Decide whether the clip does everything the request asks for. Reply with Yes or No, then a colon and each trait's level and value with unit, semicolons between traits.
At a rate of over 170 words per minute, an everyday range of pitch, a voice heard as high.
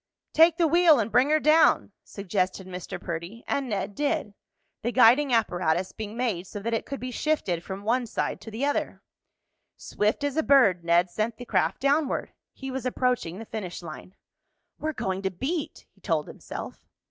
No: average, 180 wpm; wide, 6.6 semitones; high, 230 Hz